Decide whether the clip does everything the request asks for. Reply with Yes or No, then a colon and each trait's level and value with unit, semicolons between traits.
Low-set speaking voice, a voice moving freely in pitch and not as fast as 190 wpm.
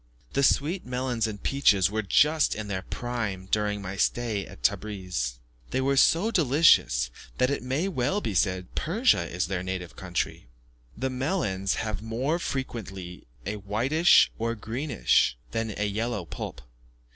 Yes: low, 110 Hz; wide, 5.7 semitones; average, 150 wpm